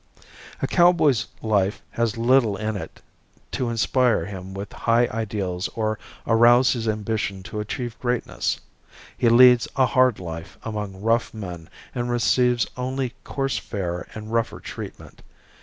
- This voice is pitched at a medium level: No, low, 115 Hz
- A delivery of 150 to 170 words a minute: No, average, 140 wpm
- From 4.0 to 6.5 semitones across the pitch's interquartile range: No, average, 3.3 semitones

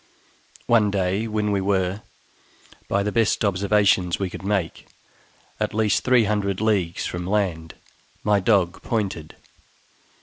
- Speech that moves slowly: Yes, slow, 130 wpm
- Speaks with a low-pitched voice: Yes, low, 100 Hz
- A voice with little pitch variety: Yes, narrow, 2.3 semitones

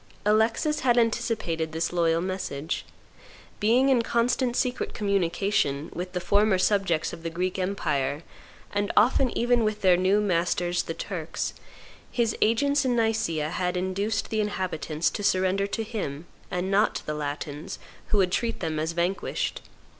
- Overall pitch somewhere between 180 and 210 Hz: Yes, high, 190 Hz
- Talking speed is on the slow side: No, average, 155 wpm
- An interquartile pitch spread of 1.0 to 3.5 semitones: No, average, 4.8 semitones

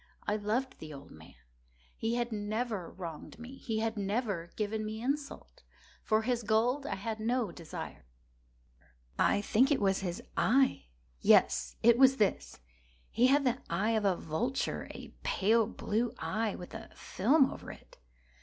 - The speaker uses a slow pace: No, average, 155 wpm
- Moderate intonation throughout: Yes, average, 3.5 semitones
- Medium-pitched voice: No, high, 220 Hz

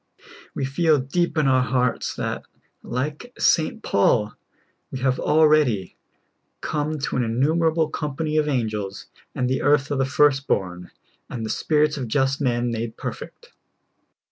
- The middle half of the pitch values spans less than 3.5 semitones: No, average, 3.9 semitones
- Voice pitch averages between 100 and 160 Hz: Yes, low, 135 Hz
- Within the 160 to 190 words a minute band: No, average, 150 wpm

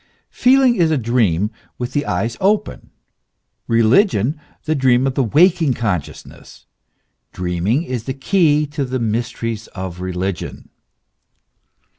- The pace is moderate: No, slow, 120 wpm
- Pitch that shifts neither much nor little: No, wide, 6.0 semitones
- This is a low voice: Yes, low, 125 Hz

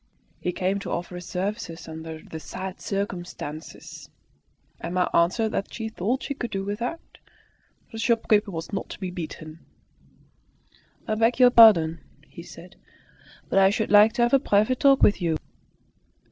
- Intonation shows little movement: No, average, 4.3 semitones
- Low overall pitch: No, high, 200 Hz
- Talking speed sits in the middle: Yes, average, 160 wpm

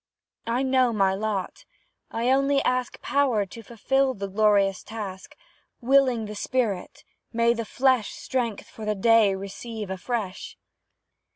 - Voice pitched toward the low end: No, high, 225 Hz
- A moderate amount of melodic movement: Yes, average, 4.0 semitones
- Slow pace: Yes, slow, 130 wpm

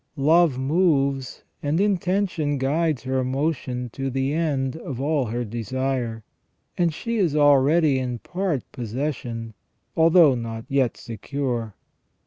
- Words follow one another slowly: Yes, slow, 120 wpm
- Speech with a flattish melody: No, average, 4.2 semitones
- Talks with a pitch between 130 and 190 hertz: Yes, low, 135 Hz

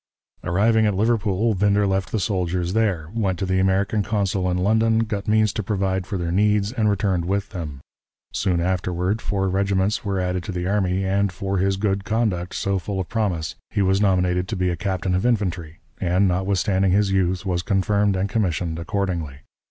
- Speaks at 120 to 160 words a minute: No, average, 190 wpm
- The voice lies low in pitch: Yes, very low, 95 Hz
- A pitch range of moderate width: No, narrow, 2.1 semitones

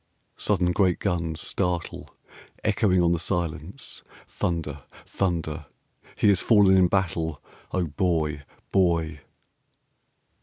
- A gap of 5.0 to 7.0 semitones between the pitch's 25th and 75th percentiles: No, average, 2.9 semitones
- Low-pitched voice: Yes, very low, 85 Hz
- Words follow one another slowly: Yes, slow, 105 wpm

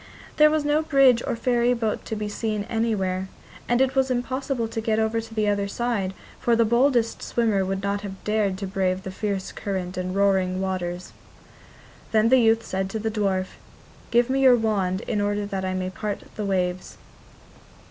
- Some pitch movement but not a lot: Yes, average, 3.7 semitones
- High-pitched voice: Yes, high, 210 Hz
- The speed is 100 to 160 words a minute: No, average, 190 wpm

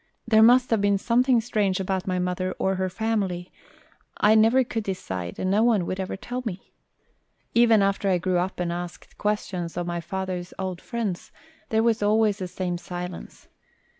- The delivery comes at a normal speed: Yes, average, 180 wpm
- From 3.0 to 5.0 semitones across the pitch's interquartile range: Yes, average, 3.5 semitones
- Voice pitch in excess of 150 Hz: Yes, high, 190 Hz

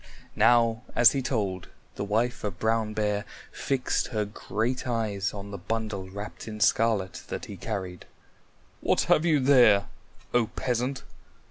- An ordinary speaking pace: Yes, average, 145 wpm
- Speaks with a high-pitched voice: No, low, 110 Hz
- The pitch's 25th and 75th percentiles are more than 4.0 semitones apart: No, average, 3.1 semitones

